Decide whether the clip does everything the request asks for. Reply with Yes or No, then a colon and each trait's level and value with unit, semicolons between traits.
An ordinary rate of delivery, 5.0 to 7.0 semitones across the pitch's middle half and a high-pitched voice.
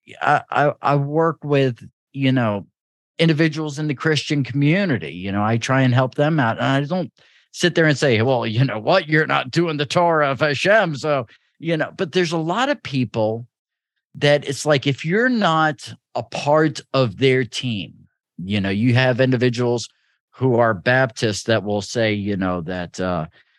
No: average, 185 wpm; average, 5.3 semitones; low, 135 Hz